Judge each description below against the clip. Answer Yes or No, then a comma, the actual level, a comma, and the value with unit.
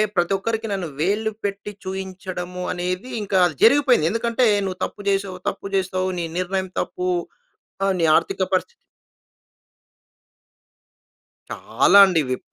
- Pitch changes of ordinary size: No, narrow, 2.2 semitones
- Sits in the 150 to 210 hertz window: Yes, high, 190 Hz